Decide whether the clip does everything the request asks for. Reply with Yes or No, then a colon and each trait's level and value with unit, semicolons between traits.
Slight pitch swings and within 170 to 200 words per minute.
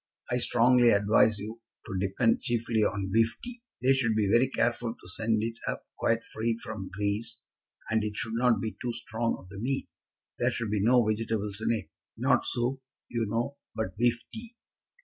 Yes: narrow, 2.2 semitones; average, 190 wpm